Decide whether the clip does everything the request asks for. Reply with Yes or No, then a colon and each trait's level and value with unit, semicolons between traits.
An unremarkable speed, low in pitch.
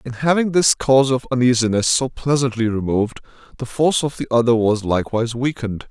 Yes: average, 175 wpm; low, 125 Hz